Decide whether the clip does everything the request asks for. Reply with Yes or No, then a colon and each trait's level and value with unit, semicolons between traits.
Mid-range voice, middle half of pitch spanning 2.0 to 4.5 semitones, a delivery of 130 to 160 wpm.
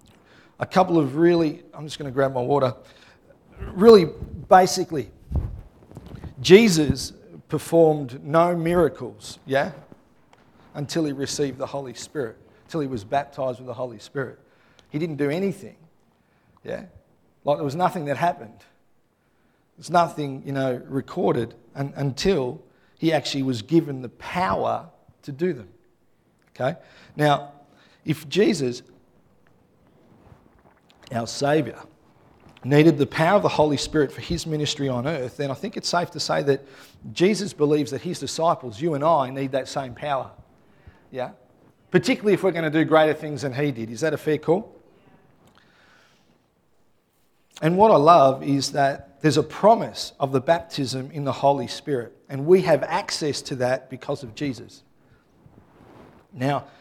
Yes: medium, 145 Hz; average, 3.5 semitones; average, 150 wpm